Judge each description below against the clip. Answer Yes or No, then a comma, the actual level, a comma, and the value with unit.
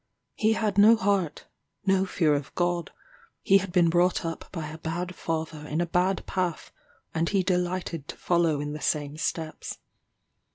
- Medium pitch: Yes, medium, 175 Hz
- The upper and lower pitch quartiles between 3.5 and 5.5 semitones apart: No, average, 2.8 semitones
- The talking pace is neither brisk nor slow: Yes, average, 170 wpm